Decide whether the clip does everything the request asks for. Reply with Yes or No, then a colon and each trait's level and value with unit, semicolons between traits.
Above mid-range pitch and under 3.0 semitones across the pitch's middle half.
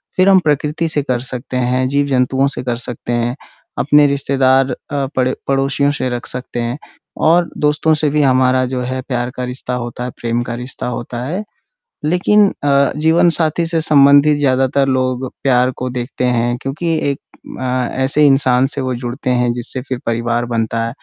No: low, 130 Hz; narrow, 2.6 semitones